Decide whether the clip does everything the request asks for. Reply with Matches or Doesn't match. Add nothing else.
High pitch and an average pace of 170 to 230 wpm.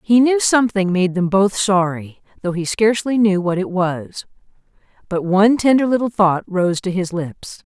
Matches